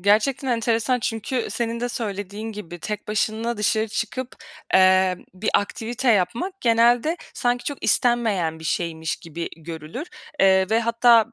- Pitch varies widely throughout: No, average, 4.0 semitones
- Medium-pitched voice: No, high, 220 Hz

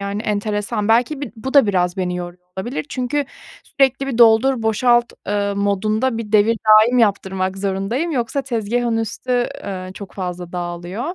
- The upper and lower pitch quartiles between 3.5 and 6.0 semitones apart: Yes, average, 3.9 semitones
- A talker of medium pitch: No, high, 215 Hz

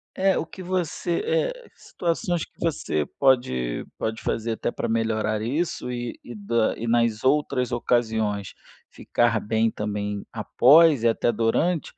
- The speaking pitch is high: No, low, 120 Hz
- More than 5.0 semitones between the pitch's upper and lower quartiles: Yes, wide, 5.4 semitones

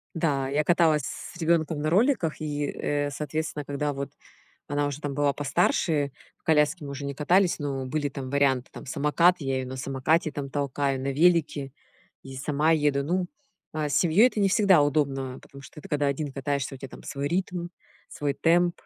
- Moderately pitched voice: Yes, medium, 145 Hz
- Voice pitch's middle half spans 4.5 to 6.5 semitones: No, narrow, 2.6 semitones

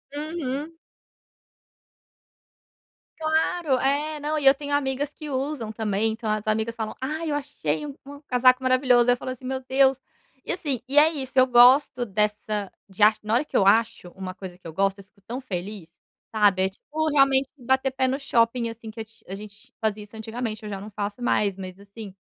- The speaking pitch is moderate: No, high, 245 Hz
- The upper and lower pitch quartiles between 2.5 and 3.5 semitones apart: No, average, 4.5 semitones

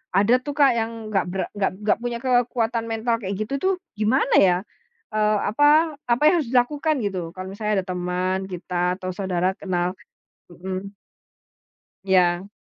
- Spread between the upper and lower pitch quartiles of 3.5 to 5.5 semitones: Yes, average, 4.2 semitones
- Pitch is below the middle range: No, high, 205 Hz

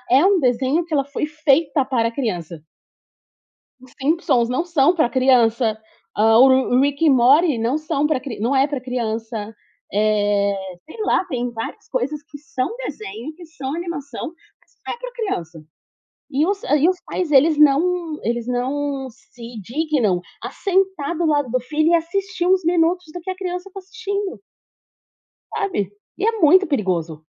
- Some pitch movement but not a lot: No, wide, 6.2 semitones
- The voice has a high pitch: Yes, very high, 280 Hz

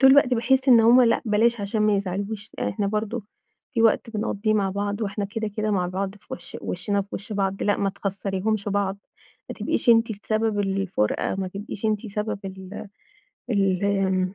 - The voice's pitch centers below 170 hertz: No, high, 205 Hz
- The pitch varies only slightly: Yes, narrow, 2.0 semitones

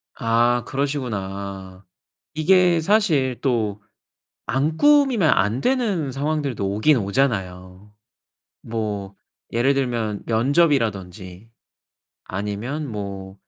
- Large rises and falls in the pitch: Yes, wide, 6.6 semitones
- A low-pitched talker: Yes, low, 120 Hz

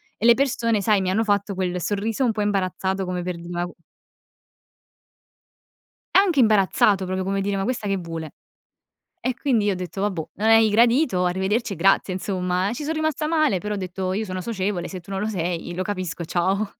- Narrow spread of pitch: No, average, 3.1 semitones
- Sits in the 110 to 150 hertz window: No, high, 195 Hz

